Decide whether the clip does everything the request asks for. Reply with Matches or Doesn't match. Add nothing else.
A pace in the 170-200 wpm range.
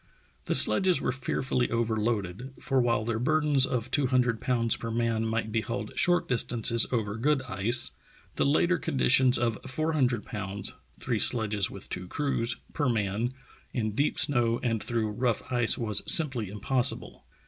Doesn't match